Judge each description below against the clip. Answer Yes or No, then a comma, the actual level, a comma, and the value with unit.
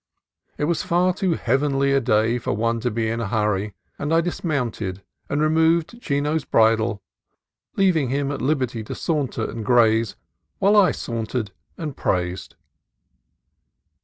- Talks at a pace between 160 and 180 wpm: No, average, 145 wpm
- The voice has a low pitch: Yes, low, 130 Hz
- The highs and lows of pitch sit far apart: Yes, wide, 5.8 semitones